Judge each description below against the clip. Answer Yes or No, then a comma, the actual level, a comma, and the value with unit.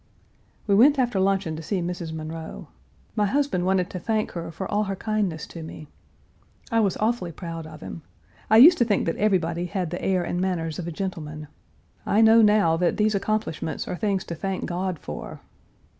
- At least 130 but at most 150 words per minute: No, average, 195 wpm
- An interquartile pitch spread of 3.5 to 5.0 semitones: Yes, average, 4.2 semitones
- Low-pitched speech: No, medium, 185 Hz